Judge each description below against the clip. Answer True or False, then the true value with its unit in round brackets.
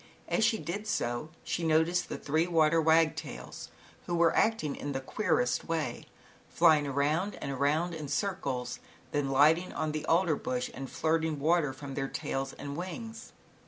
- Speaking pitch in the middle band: True (155 Hz)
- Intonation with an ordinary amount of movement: True (3.6 semitones)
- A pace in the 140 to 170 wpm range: True (160 wpm)